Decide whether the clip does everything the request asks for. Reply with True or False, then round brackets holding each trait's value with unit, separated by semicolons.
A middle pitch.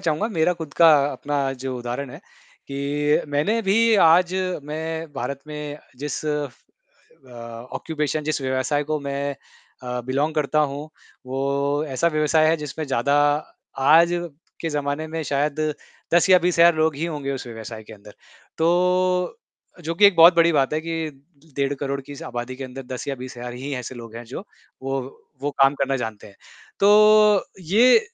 True (145 Hz)